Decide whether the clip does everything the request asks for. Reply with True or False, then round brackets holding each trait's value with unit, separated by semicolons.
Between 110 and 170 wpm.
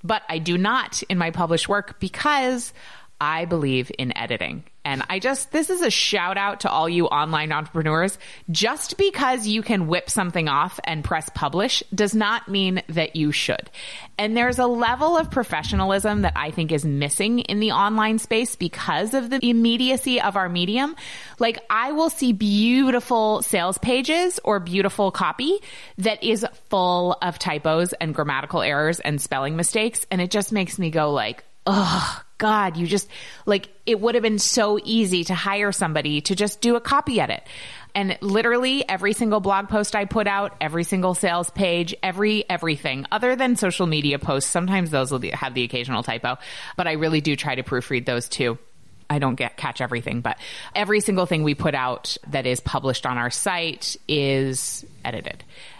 False (180 wpm)